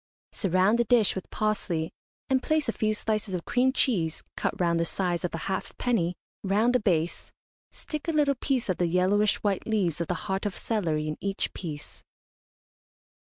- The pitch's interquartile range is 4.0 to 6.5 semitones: Yes, average, 4.8 semitones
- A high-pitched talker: Yes, high, 195 Hz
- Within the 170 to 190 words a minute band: Yes, average, 180 wpm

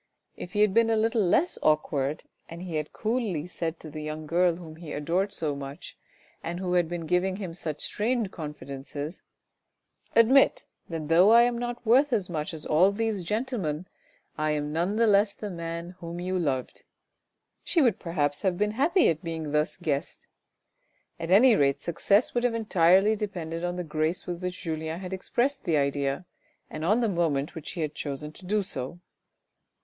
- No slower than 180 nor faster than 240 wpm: Yes, average, 190 wpm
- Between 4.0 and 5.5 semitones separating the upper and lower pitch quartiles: Yes, average, 5.1 semitones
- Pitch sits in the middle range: Yes, medium, 175 Hz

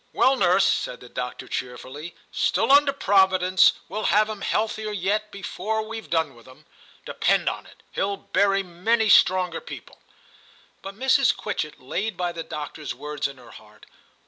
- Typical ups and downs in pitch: No, wide, 5.9 semitones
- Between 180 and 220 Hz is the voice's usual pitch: Yes, high, 190 Hz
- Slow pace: No, average, 160 wpm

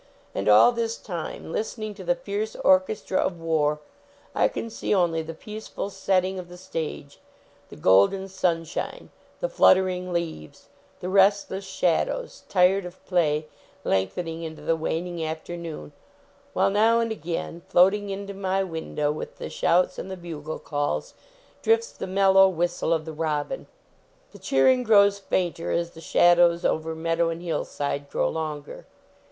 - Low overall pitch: No, medium, 175 Hz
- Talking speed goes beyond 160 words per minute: No, average, 150 wpm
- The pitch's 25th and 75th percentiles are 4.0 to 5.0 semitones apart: No, average, 3.3 semitones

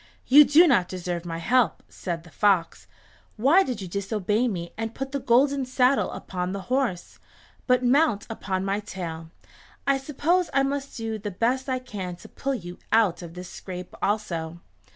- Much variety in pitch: Yes, wide, 6.6 semitones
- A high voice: Yes, high, 215 Hz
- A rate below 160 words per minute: No, average, 175 wpm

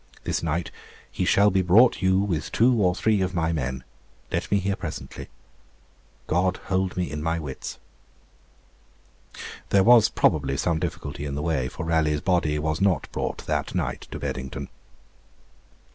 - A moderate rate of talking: Yes, average, 160 wpm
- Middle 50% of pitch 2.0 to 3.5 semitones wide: No, average, 4.0 semitones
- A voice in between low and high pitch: No, very low, 85 Hz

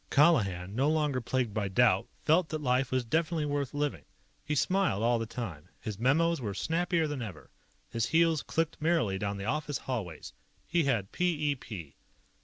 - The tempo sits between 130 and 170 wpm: No, average, 180 wpm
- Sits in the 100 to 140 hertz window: Yes, low, 135 Hz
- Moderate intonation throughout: No, wide, 6.4 semitones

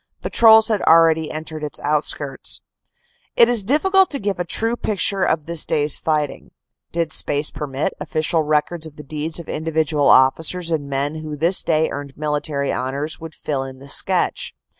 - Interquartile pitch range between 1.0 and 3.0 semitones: Yes, average, 2.7 semitones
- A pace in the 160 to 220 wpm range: Yes, average, 170 wpm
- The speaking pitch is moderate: Yes, medium, 155 Hz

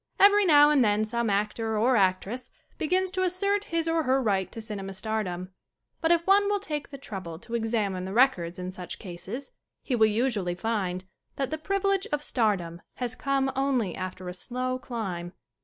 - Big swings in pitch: Yes, wide, 7.5 semitones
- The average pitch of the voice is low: No, high, 230 Hz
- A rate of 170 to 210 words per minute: Yes, average, 195 wpm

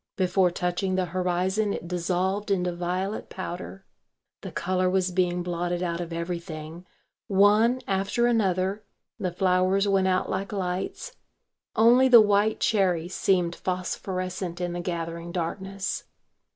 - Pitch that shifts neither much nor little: No, narrow, 1.9 semitones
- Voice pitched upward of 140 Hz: Yes, medium, 185 Hz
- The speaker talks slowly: Yes, slow, 130 wpm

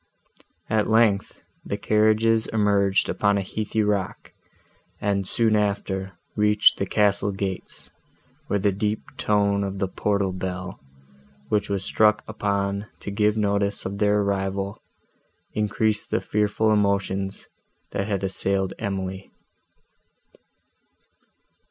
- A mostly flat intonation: Yes, narrow, 1.3 semitones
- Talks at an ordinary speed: No, slow, 115 wpm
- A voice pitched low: Yes, low, 100 Hz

